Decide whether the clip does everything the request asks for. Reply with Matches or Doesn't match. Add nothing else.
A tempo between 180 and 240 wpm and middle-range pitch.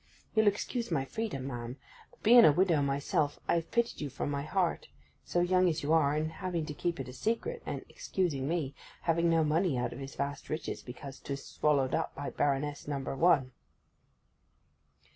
Matches